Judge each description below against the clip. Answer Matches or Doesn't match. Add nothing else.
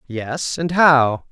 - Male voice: Matches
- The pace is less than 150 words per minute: Matches